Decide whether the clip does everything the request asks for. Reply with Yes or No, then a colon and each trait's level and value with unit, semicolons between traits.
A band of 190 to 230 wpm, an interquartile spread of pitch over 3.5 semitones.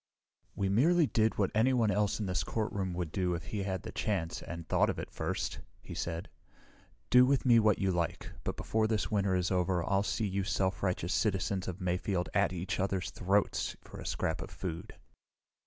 No: average, 200 wpm; average, 3.0 semitones